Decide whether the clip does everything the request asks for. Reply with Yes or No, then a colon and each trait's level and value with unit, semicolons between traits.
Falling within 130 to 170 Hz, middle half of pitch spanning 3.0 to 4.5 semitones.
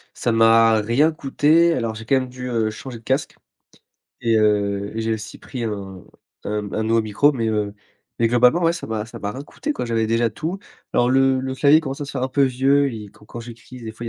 No: low, 115 Hz; average, 3.4 semitones